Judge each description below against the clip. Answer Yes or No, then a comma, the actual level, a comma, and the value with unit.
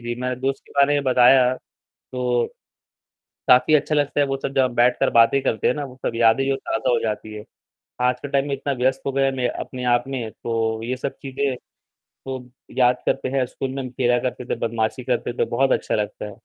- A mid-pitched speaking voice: No, low, 125 Hz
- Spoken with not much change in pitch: Yes, narrow, 2.2 semitones